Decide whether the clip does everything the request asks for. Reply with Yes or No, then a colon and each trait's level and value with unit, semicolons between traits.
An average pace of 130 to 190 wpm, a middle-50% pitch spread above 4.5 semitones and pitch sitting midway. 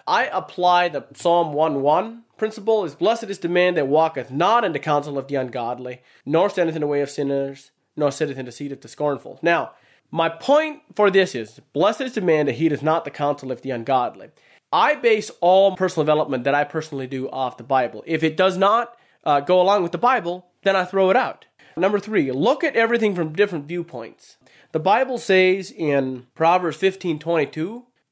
No: fast, 205 wpm; average, 5.2 semitones; medium, 165 Hz